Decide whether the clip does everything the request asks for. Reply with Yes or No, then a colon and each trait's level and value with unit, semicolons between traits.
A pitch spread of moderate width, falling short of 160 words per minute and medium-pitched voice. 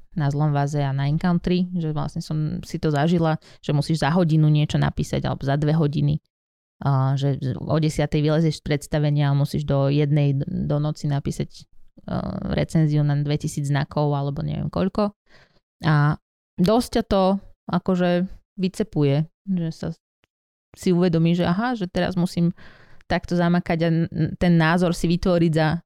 Yes: average, 3.1 semitones; average, 150 wpm; medium, 160 Hz